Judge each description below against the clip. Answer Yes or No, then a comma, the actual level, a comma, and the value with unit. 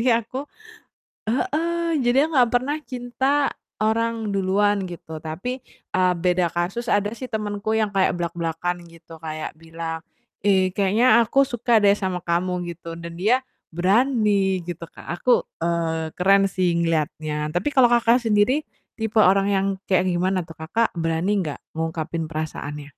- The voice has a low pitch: No, high, 190 Hz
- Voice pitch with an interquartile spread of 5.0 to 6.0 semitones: Yes, wide, 5.4 semitones